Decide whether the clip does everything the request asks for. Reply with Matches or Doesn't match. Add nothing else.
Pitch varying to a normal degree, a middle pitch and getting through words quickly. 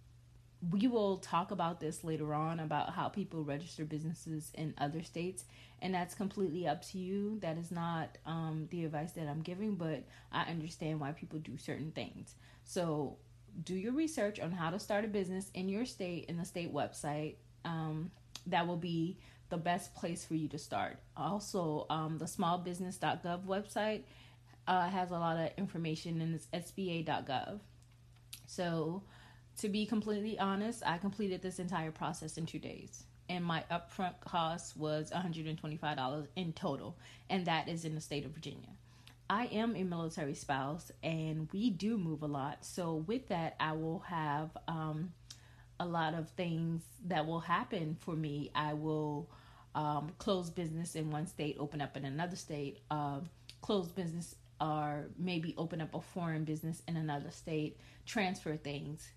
Doesn't match